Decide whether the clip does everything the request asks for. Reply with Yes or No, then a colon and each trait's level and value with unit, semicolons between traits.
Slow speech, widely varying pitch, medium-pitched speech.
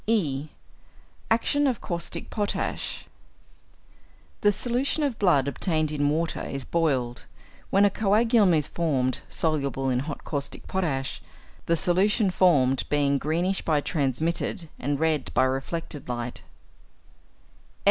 Yes: slow, 120 wpm; wide, 5.8 semitones; medium, 160 Hz